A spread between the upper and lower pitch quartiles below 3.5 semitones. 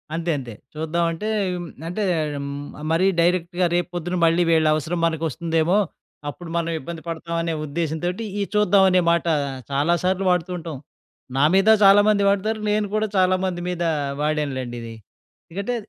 Yes: narrow, 2.6 semitones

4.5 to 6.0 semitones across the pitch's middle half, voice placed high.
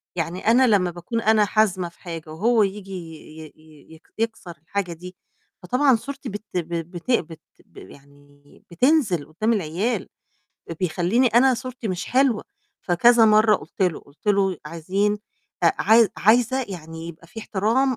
Yes: average, 5.1 semitones; high, 195 Hz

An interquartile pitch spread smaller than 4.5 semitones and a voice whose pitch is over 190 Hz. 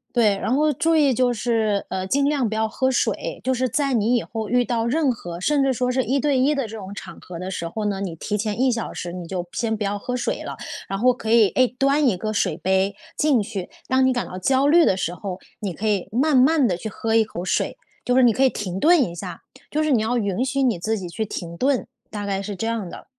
No: average, 4.8 semitones; high, 225 Hz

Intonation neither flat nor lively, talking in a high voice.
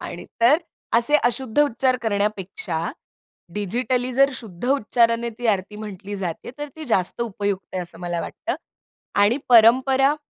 Yes: average, 4.1 semitones; high, 225 Hz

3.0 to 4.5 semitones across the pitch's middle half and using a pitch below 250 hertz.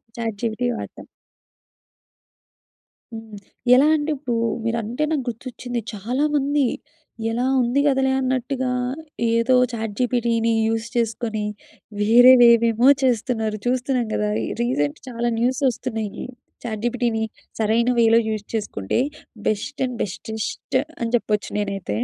No: narrow, 2.4 semitones; high, 235 Hz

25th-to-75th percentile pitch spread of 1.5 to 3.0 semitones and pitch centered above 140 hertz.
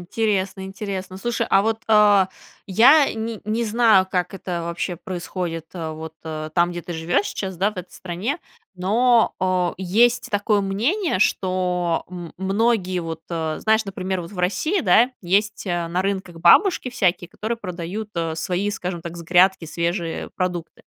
No: average, 3.5 semitones; medium, 185 Hz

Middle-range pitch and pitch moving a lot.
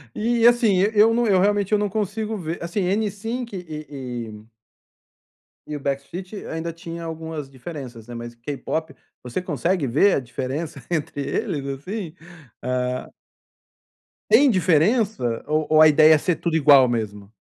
Yes: medium, 160 Hz; wide, 6.6 semitones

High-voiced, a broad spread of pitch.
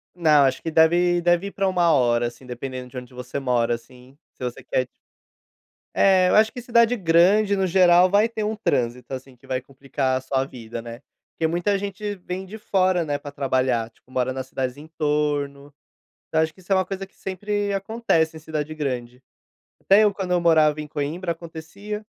No: medium, 160 Hz; wide, 6.4 semitones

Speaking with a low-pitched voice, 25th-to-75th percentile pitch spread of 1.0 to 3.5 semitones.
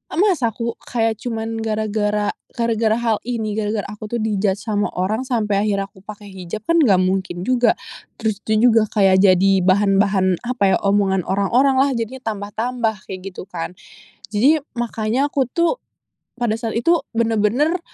No: high, 215 Hz; average, 3.0 semitones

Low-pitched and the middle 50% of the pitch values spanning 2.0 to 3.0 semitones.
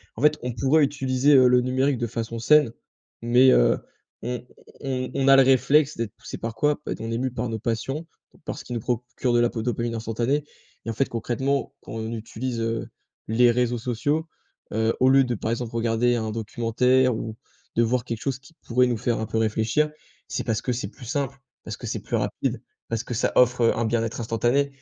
Yes: low, 120 Hz; narrow, 2.5 semitones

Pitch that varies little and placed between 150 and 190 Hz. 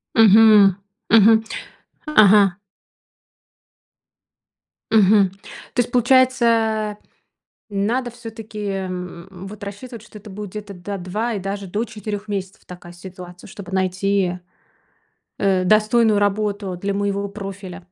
No: narrow, 2.3 semitones; high, 205 Hz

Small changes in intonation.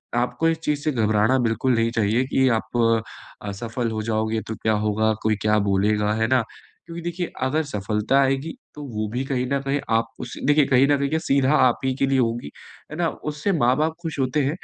No: average, 4.5 semitones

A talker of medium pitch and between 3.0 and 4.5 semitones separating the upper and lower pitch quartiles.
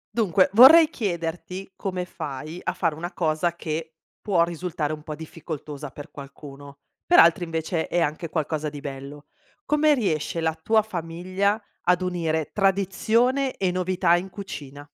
Yes: medium, 170 Hz; average, 3.8 semitones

